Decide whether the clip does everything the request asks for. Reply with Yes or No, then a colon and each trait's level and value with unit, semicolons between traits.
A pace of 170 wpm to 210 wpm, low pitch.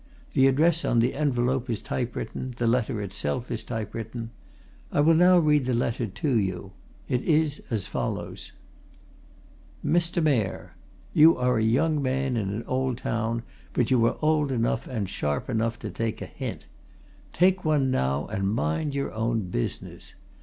No: average, 160 wpm; low, 125 Hz